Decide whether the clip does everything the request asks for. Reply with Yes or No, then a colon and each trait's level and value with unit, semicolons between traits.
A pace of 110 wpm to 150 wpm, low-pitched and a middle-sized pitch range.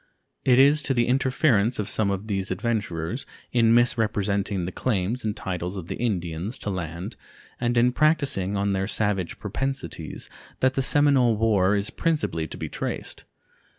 No: average, 160 wpm; low, 105 Hz; average, 4.5 semitones